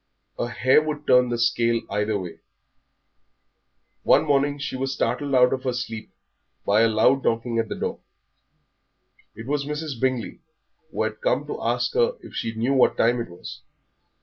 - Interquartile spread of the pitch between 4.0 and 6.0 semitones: No, average, 3.3 semitones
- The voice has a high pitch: No, low, 125 Hz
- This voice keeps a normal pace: Yes, average, 175 wpm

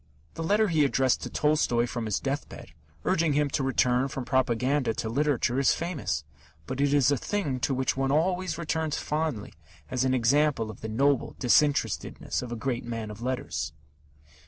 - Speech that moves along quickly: No, average, 180 wpm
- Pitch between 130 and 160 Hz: Yes, low, 135 Hz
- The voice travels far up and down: No, average, 3.6 semitones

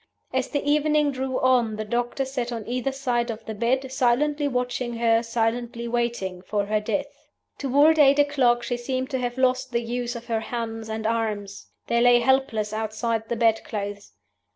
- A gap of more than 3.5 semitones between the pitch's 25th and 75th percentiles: No, average, 2.7 semitones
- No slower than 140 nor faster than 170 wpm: No, average, 180 wpm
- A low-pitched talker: No, high, 240 Hz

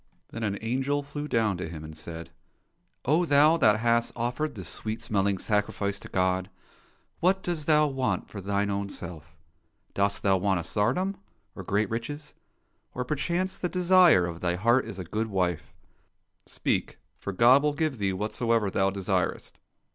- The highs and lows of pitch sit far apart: Yes, wide, 7.0 semitones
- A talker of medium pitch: No, low, 110 Hz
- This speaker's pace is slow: No, average, 170 wpm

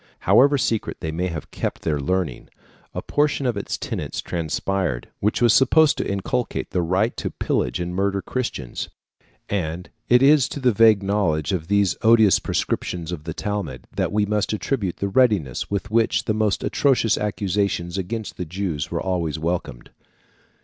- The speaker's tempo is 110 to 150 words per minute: No, average, 170 wpm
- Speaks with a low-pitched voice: Yes, low, 100 Hz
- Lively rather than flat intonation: No, average, 4.3 semitones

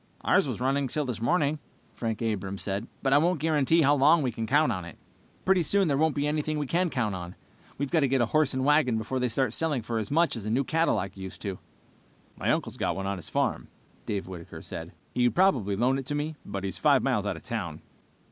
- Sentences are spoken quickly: Yes, fast, 245 wpm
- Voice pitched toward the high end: No, low, 130 Hz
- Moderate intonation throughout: No, wide, 5.8 semitones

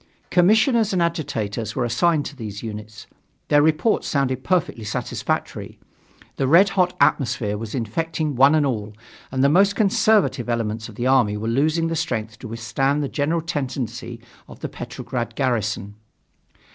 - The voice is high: No, low, 135 Hz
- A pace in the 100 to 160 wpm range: Yes, average, 155 wpm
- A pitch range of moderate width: No, wide, 6.3 semitones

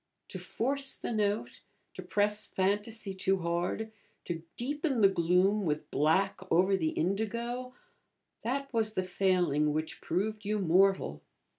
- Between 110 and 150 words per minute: Yes, slow, 135 wpm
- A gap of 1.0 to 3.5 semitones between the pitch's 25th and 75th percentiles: No, average, 3.9 semitones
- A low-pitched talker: No, high, 195 Hz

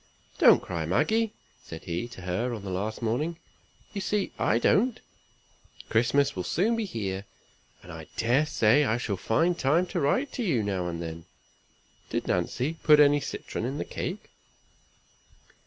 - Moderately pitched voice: No, low, 125 Hz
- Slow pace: No, average, 165 wpm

